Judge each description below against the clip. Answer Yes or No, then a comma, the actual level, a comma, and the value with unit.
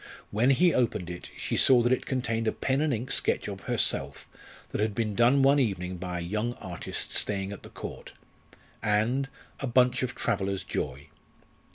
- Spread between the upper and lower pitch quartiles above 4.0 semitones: Yes, average, 4.8 semitones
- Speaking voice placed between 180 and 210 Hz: No, low, 115 Hz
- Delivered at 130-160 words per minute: No, average, 185 wpm